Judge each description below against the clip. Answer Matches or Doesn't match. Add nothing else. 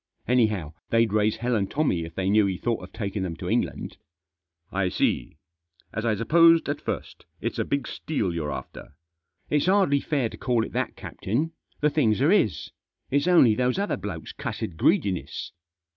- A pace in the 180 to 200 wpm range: Matches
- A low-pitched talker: Matches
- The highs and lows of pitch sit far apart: Matches